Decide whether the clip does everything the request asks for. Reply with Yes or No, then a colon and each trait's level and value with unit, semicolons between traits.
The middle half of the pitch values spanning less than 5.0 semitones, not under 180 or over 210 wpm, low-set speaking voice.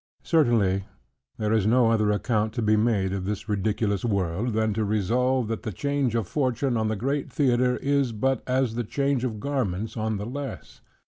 Yes: average, 3.4 semitones; average, 190 wpm; low, 115 Hz